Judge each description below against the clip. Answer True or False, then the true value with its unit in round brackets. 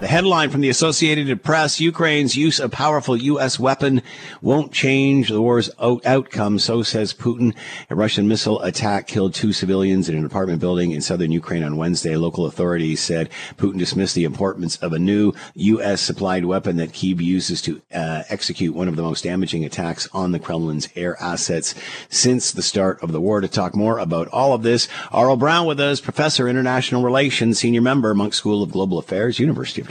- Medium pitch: False (105 Hz)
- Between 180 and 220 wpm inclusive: True (195 wpm)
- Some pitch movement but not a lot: False (6.8 semitones)